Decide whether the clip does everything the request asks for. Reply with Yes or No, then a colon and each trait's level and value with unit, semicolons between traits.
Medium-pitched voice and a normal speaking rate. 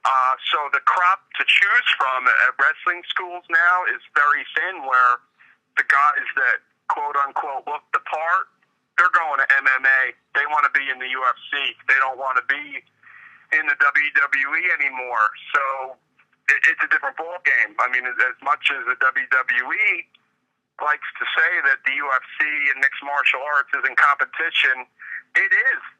Yes: medium, 145 Hz; average, 170 wpm